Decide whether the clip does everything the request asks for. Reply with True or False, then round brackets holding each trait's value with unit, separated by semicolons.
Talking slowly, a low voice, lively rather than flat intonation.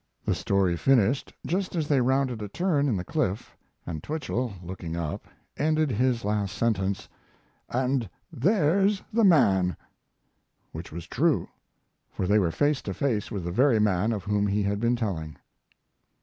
False (160 wpm; 110 Hz; 6.4 semitones)